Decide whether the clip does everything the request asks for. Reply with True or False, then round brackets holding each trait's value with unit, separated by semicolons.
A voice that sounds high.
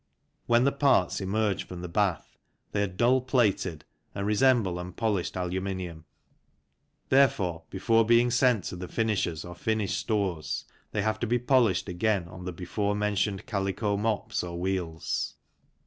False (100 Hz)